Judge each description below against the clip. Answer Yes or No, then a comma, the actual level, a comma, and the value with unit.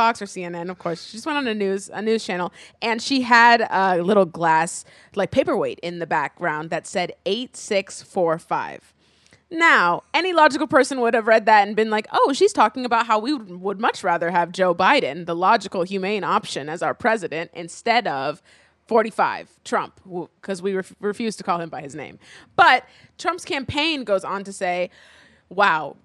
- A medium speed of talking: Yes, average, 180 wpm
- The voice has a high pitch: Yes, high, 200 Hz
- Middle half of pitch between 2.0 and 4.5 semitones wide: No, average, 4.9 semitones